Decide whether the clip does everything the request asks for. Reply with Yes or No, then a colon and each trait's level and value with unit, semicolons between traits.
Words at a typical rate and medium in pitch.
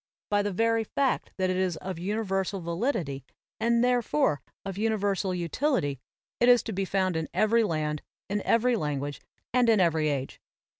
No: average, 165 wpm; high, 195 Hz